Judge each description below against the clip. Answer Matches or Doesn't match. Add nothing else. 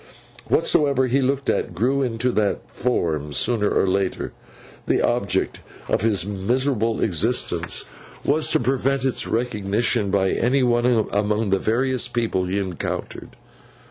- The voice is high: Doesn't match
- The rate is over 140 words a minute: Doesn't match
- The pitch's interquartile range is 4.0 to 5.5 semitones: Matches